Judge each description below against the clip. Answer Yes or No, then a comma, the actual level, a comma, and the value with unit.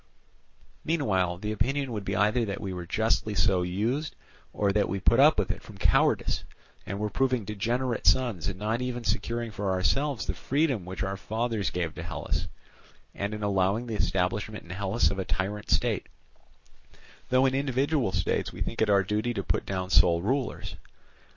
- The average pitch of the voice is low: Yes, low, 105 Hz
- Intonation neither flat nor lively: Yes, average, 4.2 semitones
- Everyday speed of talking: Yes, average, 185 wpm